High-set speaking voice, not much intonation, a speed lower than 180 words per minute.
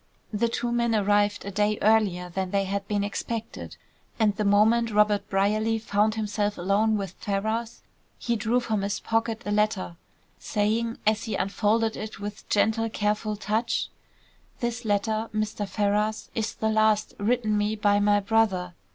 Yes: high, 210 Hz; narrow, 1.5 semitones; average, 160 wpm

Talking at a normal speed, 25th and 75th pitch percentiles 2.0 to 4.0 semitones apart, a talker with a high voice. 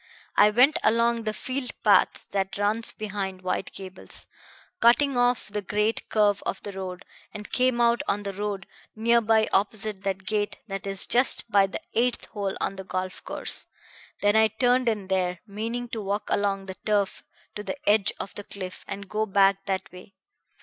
Yes: average, 180 wpm; narrow, 2.5 semitones; high, 205 Hz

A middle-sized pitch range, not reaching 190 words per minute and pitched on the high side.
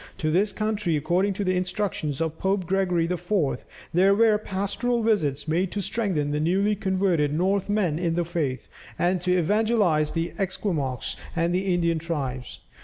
No: average, 3.6 semitones; average, 160 wpm; medium, 180 Hz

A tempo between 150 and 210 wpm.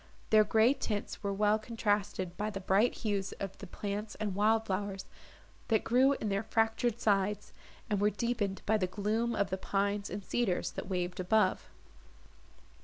Yes: average, 170 wpm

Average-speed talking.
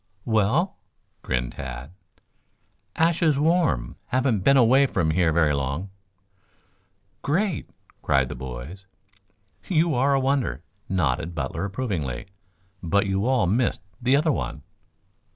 No: slow, 115 wpm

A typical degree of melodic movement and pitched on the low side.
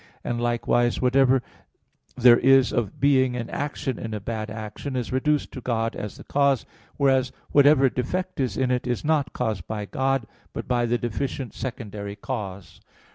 Yes: average, 3.0 semitones; low, 125 Hz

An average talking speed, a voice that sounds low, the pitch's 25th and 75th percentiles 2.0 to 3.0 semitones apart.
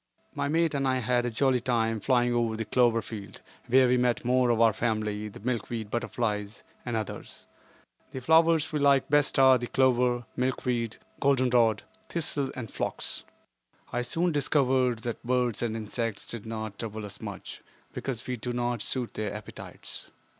Yes: average, 170 wpm; low, 120 Hz; narrow, 2.5 semitones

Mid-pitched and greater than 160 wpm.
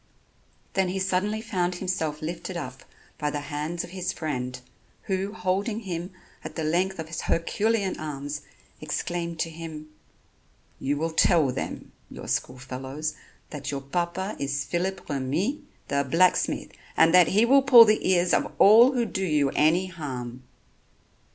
No: medium, 170 Hz; average, 155 wpm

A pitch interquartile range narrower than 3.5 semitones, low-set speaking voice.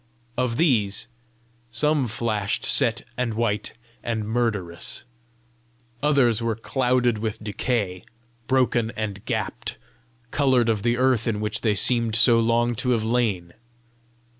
Yes: narrow, 2.5 semitones; low, 115 Hz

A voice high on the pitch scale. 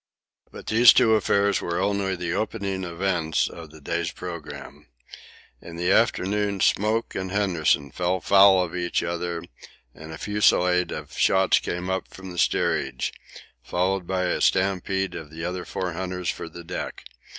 No: very low, 90 Hz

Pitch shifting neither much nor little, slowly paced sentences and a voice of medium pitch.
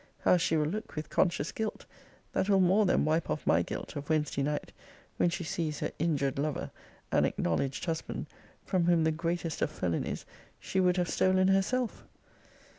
No: average, 3.8 semitones; average, 180 wpm; medium, 165 Hz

